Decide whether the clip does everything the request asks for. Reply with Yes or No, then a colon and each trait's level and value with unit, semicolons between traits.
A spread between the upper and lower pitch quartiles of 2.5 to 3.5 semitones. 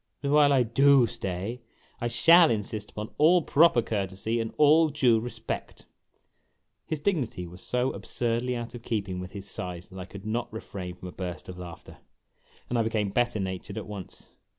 No: average, 4.6 semitones